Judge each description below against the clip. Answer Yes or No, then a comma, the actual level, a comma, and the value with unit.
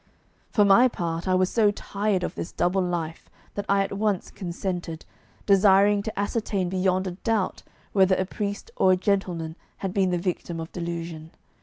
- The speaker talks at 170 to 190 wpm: Yes, average, 175 wpm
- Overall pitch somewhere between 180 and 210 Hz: Yes, high, 190 Hz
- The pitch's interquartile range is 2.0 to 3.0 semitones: Yes, narrow, 2.4 semitones